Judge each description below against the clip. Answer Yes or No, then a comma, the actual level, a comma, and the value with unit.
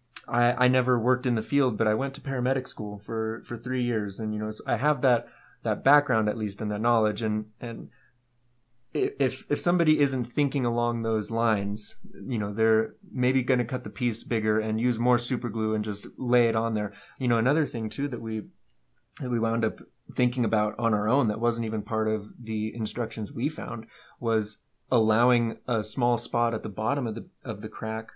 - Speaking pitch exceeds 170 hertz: No, low, 115 Hz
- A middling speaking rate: No, fast, 210 wpm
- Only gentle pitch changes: Yes, narrow, 2.3 semitones